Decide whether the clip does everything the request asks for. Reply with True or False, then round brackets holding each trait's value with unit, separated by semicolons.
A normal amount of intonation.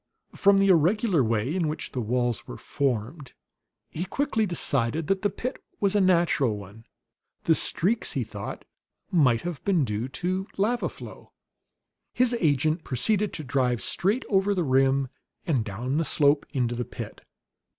False (7.4 semitones)